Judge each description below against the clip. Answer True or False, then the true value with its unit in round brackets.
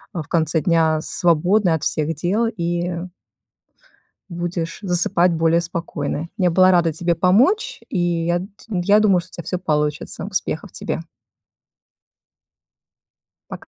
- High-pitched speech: False (175 Hz)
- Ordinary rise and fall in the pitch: False (2.2 semitones)